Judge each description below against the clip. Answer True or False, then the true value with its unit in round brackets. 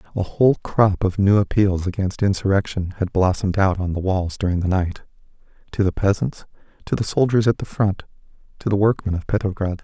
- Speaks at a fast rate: False (185 wpm)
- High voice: False (100 Hz)